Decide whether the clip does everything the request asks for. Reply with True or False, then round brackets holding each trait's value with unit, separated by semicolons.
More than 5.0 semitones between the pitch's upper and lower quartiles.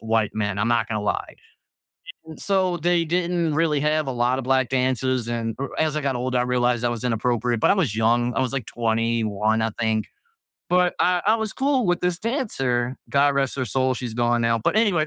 True (5.6 semitones)